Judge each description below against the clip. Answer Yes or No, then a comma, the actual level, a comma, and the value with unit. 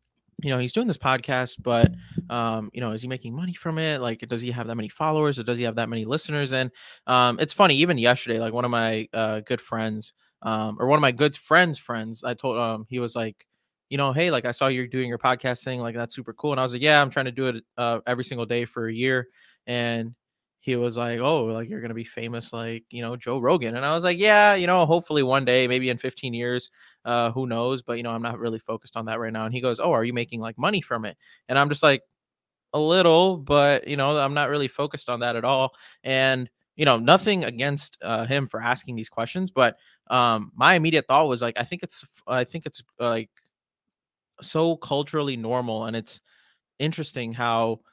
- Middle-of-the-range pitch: No, low, 125 Hz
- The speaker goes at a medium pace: No, fast, 240 wpm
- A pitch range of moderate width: Yes, average, 3.6 semitones